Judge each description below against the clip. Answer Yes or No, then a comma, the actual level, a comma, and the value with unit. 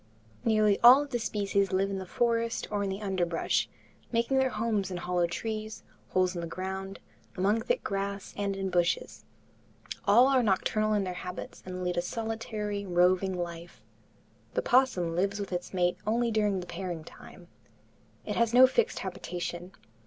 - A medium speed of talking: Yes, average, 170 wpm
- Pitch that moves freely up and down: No, average, 3.5 semitones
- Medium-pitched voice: No, high, 195 Hz